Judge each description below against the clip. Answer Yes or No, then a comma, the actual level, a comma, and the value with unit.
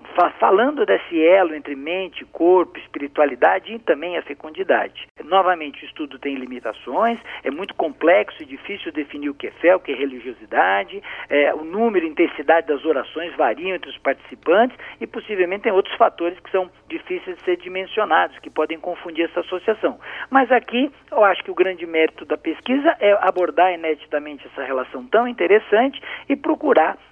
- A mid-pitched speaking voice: Yes, medium, 180 Hz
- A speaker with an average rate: Yes, average, 170 wpm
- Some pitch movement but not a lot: No, wide, 6.9 semitones